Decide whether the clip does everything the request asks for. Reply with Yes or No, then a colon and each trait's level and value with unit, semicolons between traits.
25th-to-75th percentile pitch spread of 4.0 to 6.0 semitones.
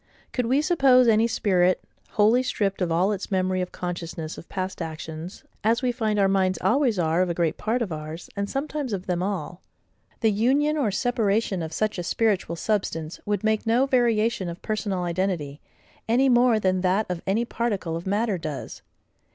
Yes: average, 4.6 semitones